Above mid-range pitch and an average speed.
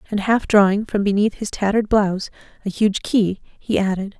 Yes: high, 205 Hz; average, 185 wpm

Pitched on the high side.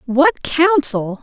Yes: very high, 280 Hz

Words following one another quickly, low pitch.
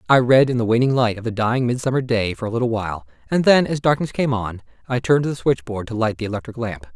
Yes: fast, 275 wpm; low, 120 Hz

